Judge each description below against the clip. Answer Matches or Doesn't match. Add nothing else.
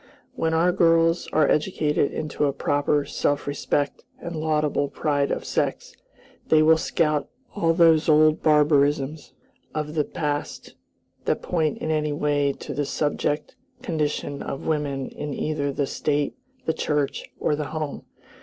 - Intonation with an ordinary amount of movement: Doesn't match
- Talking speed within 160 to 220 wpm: Doesn't match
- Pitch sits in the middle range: Matches